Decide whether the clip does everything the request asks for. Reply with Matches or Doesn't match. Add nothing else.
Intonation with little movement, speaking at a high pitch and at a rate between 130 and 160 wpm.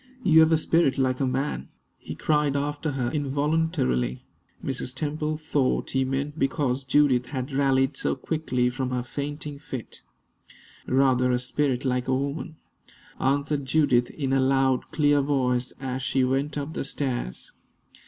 Doesn't match